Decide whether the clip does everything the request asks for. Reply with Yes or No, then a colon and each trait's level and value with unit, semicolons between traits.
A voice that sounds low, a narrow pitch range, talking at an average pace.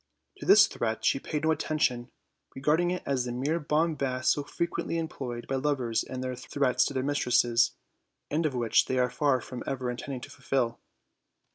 No: low, 130 Hz; average, 3.1 semitones; average, 175 wpm